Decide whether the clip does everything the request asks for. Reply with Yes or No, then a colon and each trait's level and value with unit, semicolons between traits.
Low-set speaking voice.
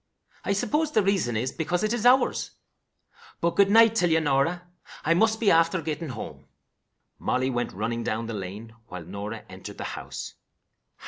No: medium, 160 Hz